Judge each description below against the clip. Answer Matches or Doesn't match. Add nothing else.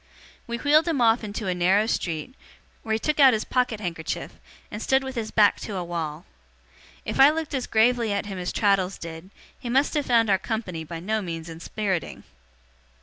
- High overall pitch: Matches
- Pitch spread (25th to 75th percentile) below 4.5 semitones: Doesn't match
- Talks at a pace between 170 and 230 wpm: Matches